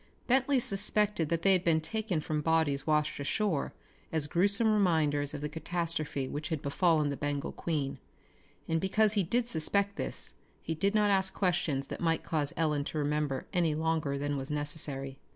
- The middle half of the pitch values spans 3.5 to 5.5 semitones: Yes, average, 4.6 semitones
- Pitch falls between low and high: Yes, medium, 160 Hz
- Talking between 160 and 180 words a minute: Yes, average, 175 wpm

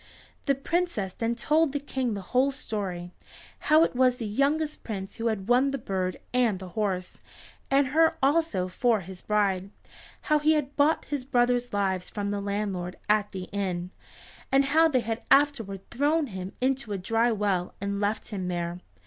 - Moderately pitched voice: No, high, 225 Hz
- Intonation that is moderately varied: No, wide, 6.0 semitones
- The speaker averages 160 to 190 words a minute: Yes, average, 180 wpm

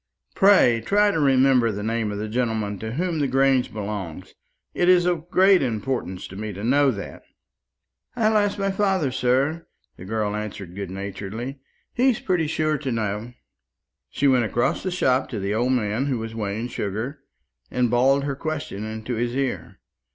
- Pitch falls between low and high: No, low, 125 Hz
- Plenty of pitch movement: Yes, wide, 5.9 semitones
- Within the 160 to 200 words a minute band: Yes, average, 175 wpm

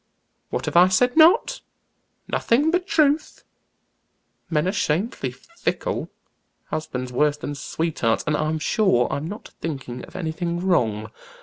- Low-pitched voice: No, medium, 165 Hz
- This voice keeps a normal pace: No, slow, 130 wpm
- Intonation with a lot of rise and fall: Yes, wide, 7.6 semitones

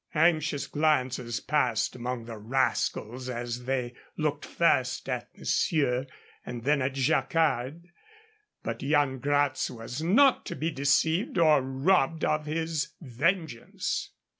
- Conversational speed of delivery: No, slow, 120 wpm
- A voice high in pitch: No, medium, 140 Hz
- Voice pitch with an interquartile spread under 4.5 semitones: Yes, average, 3.8 semitones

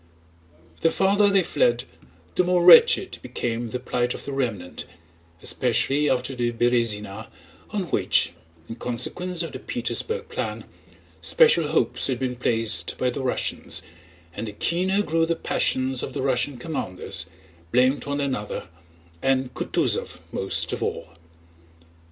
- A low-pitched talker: Yes, low, 130 Hz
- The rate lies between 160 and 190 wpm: No, average, 140 wpm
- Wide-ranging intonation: Yes, wide, 5.9 semitones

